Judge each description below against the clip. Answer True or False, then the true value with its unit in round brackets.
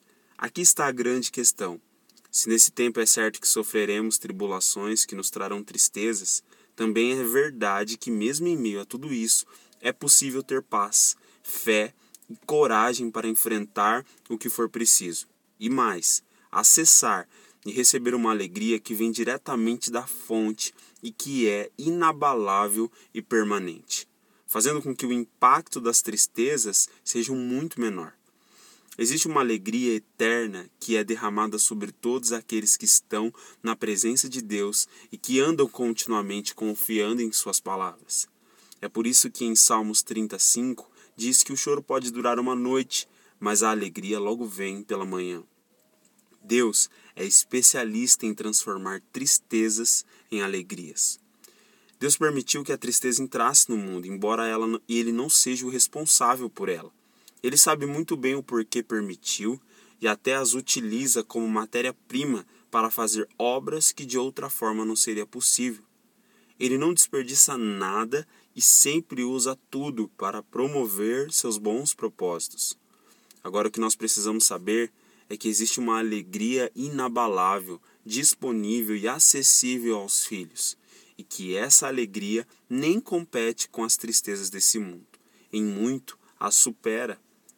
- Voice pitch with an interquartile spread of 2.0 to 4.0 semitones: True (2.8 semitones)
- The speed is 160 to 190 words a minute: False (140 wpm)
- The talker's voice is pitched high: False (115 Hz)